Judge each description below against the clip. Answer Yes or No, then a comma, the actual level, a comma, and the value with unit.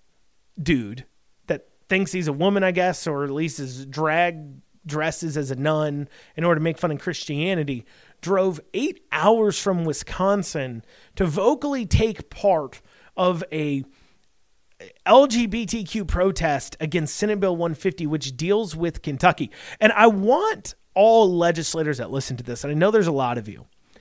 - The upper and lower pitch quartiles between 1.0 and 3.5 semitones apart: No, average, 4.7 semitones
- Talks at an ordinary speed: Yes, average, 155 wpm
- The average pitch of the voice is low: No, medium, 170 Hz